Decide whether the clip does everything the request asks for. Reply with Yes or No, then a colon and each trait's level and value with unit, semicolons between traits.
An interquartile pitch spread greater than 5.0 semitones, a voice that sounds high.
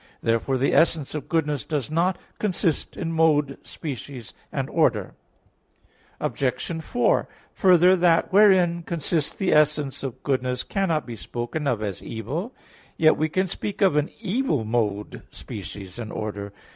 No: wide, 5.6 semitones; medium, 150 Hz